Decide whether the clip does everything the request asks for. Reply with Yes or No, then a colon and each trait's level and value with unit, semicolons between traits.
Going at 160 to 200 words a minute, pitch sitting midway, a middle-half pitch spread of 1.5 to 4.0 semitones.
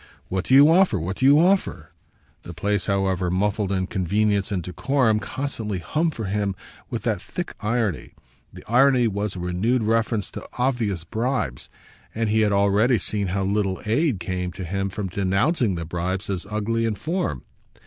No: average, 175 wpm; low, 105 Hz; average, 3.7 semitones